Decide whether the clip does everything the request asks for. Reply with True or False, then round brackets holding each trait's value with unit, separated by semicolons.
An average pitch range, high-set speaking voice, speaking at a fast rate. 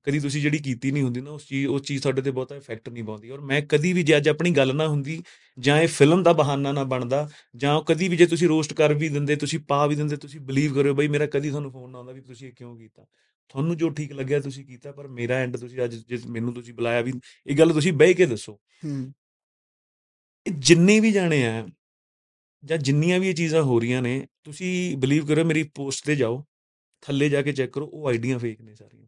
False (3.1 semitones; 140 Hz; 235 wpm)